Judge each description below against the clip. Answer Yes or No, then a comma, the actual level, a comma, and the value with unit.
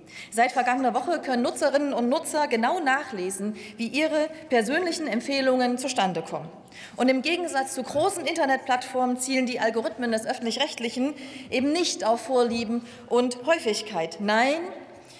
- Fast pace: No, average, 135 wpm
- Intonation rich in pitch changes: No, average, 3.7 semitones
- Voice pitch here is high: Yes, very high, 255 Hz